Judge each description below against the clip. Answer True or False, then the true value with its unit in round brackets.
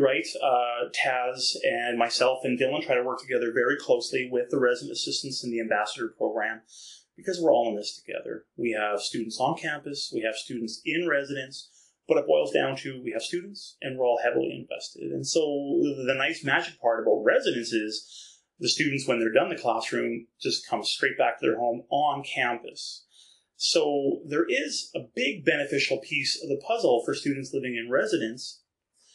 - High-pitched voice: False (125 Hz)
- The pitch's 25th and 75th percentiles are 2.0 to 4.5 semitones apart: True (3.7 semitones)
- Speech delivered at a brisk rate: False (185 wpm)